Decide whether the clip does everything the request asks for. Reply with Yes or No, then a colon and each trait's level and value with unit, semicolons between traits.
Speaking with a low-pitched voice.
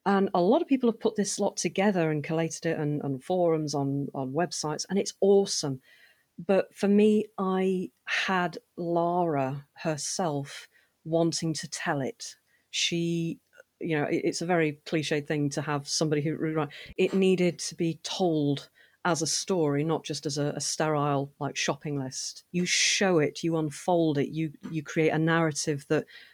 No: medium, 165 Hz